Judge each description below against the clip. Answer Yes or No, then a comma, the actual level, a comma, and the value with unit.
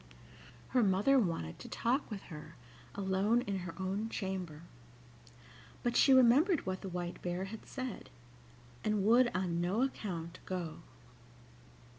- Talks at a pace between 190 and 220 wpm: No, slow, 135 wpm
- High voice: Yes, high, 195 Hz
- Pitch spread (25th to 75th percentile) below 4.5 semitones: No, average, 4.8 semitones